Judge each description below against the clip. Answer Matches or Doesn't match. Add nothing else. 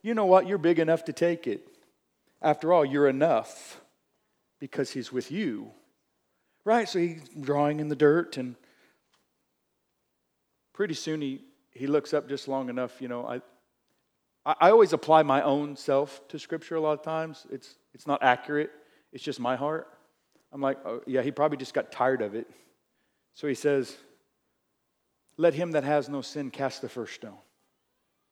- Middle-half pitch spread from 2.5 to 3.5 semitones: Matches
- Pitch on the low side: Doesn't match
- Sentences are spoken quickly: Doesn't match